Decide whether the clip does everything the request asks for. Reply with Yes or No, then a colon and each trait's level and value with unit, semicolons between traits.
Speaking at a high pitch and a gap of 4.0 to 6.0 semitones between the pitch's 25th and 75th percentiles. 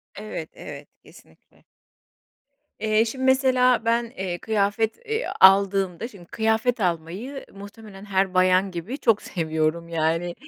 Yes: high, 200 Hz; average, 4.5 semitones